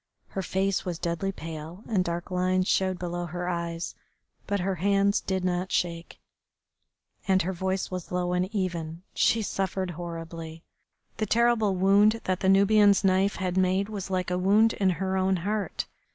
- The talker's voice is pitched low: No, medium, 185 Hz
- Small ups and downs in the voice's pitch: Yes, narrow, 1.9 semitones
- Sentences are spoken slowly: No, average, 165 wpm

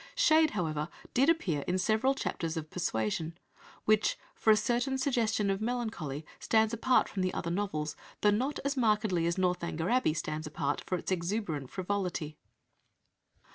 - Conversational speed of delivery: Yes, average, 155 wpm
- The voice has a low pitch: No, high, 195 Hz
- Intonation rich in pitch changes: Yes, wide, 5.9 semitones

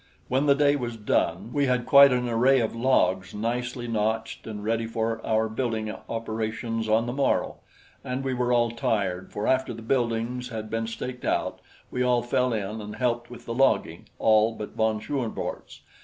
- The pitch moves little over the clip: Yes, narrow, 2.2 semitones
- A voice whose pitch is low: Yes, low, 115 Hz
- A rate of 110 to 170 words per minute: No, average, 185 wpm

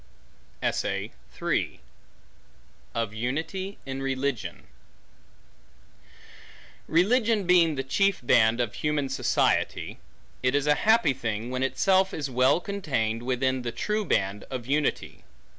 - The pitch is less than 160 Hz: Yes, low, 135 Hz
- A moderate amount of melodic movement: No, wide, 6.9 semitones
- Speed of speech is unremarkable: No, slow, 110 wpm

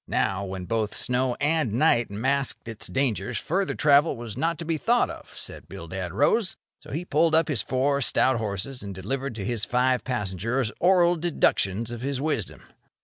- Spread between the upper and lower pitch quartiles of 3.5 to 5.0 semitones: No, wide, 5.6 semitones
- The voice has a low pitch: Yes, low, 130 Hz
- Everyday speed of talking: Yes, average, 180 wpm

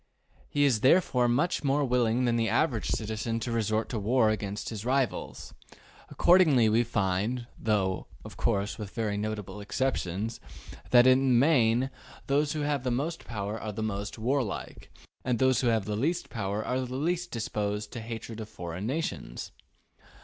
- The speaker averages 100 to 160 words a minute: Yes, average, 155 wpm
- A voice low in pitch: Yes, low, 115 Hz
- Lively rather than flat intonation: No, average, 3.6 semitones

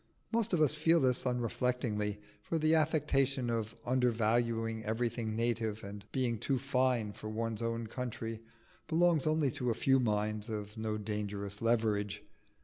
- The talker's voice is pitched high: No, low, 115 Hz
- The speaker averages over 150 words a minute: No, average, 145 wpm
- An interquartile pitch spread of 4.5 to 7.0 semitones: No, average, 3.4 semitones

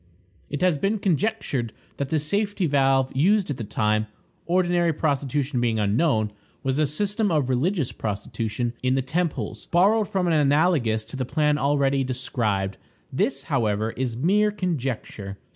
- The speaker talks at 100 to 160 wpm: Yes, average, 150 wpm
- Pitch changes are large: Yes, wide, 6.4 semitones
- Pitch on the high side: No, medium, 140 Hz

